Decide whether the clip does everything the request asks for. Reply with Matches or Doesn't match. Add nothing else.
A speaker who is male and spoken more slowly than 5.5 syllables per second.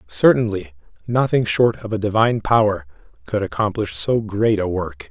Matches